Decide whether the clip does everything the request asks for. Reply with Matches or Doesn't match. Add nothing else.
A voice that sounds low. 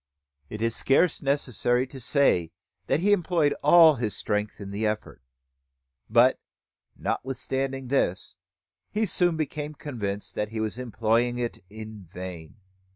Matches